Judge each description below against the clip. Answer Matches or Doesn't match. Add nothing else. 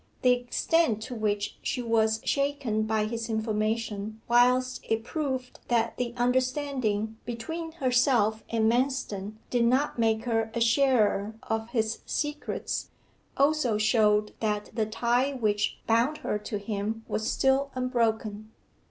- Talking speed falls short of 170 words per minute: Matches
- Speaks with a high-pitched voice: Matches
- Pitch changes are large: Doesn't match